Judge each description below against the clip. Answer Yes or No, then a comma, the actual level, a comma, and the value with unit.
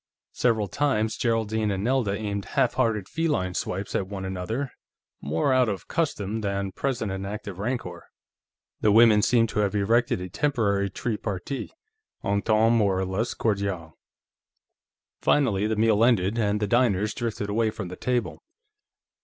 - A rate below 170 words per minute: Yes, average, 150 wpm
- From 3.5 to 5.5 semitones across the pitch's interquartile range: No, average, 2.9 semitones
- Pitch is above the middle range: No, low, 105 Hz